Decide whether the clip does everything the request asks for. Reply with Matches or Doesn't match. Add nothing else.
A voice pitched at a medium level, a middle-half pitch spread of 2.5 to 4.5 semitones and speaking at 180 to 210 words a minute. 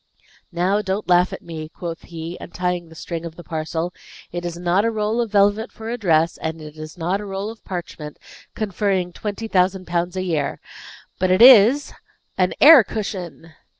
Matches